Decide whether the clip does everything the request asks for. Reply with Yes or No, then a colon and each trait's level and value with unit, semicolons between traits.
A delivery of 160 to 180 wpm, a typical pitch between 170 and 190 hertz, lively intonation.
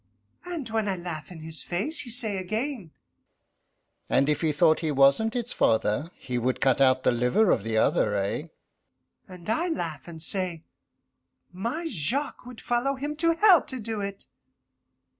Yes: average, 170 wpm; medium, 185 Hz; wide, 8.5 semitones